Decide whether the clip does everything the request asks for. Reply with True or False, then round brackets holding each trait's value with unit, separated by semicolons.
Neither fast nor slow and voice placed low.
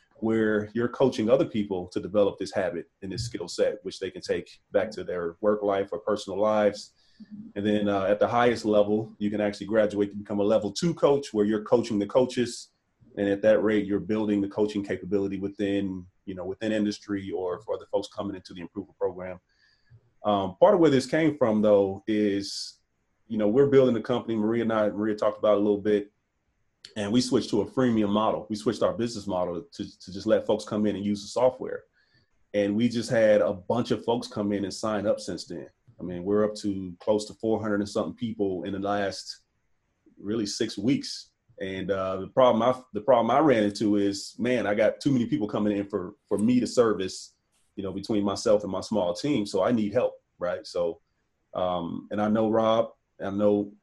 False (215 wpm; 105 Hz)